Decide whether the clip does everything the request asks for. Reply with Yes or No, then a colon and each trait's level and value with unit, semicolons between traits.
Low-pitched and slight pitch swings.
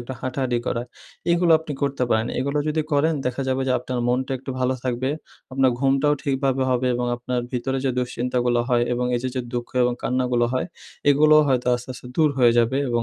Yes: low, 130 Hz; narrow, 1.8 semitones